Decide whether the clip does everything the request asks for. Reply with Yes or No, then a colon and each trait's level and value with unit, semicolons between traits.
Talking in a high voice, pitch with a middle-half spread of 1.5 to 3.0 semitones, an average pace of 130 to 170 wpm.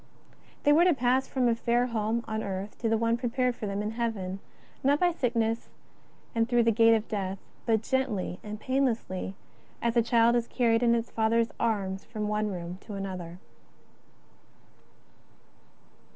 Yes: high, 230 Hz; narrow, 2.4 semitones; average, 165 wpm